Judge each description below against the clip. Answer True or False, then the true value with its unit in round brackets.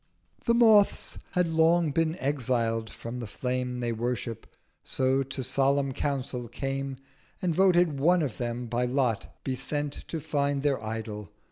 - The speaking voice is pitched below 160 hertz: True (135 Hz)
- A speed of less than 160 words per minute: True (150 wpm)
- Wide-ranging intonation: False (3.9 semitones)